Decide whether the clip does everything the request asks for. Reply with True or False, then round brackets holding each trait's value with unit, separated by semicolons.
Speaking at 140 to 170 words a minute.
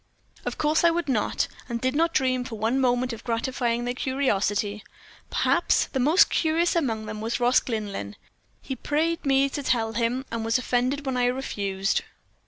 False (180 wpm)